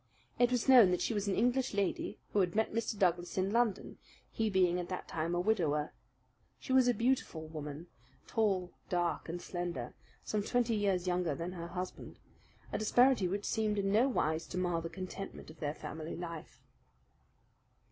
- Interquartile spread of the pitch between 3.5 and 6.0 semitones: Yes, average, 4.3 semitones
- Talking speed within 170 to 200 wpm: Yes, average, 180 wpm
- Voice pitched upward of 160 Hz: Yes, medium, 185 Hz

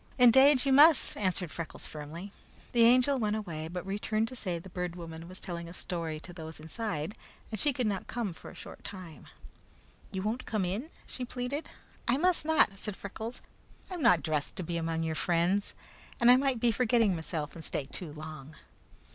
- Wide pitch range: Yes, wide, 6.4 semitones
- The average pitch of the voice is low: No, high, 190 Hz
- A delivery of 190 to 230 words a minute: Yes, average, 200 wpm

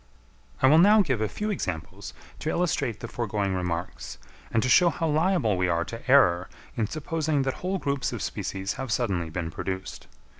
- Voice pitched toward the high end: No, low, 120 Hz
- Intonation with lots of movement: Yes, wide, 8.9 semitones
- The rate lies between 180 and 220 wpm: Yes, average, 185 wpm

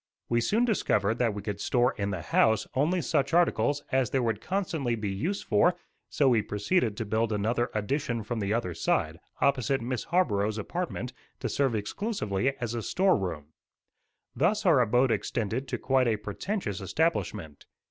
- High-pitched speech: No, low, 120 Hz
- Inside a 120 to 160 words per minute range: No, average, 170 wpm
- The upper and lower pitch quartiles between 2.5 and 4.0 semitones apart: No, average, 5.2 semitones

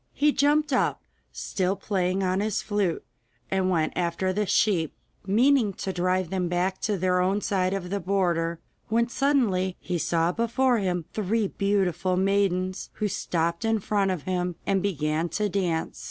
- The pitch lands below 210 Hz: Yes, high, 190 Hz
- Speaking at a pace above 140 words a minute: Yes, average, 165 wpm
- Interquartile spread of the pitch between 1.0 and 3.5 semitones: Yes, narrow, 2.6 semitones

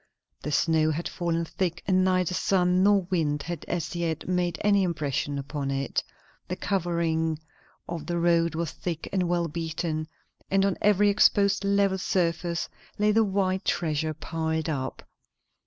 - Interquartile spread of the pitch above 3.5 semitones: No, average, 2.7 semitones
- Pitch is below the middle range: No, medium, 170 Hz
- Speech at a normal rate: Yes, average, 155 wpm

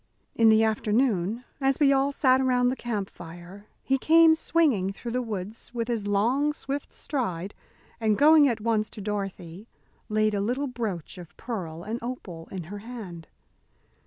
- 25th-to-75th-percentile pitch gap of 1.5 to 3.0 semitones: No, average, 4.5 semitones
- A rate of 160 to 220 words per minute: Yes, average, 165 wpm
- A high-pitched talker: Yes, high, 225 Hz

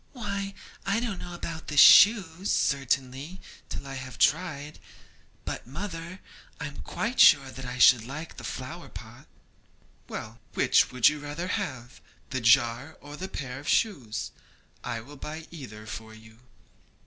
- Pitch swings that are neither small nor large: No, wide, 5.7 semitones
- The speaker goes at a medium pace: Yes, average, 155 wpm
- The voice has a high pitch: No, medium, 145 Hz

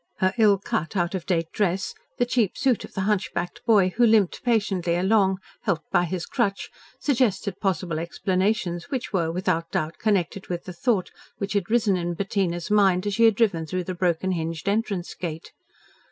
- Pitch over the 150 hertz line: Yes, high, 190 Hz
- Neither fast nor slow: Yes, average, 185 wpm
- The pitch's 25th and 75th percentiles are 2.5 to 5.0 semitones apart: Yes, average, 3.3 semitones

